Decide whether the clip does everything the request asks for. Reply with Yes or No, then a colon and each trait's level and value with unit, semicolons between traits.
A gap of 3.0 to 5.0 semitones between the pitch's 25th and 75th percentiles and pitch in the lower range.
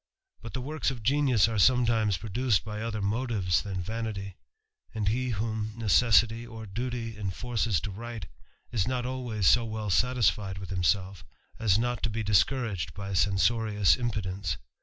Yes: average, 3.3 semitones; low, 110 Hz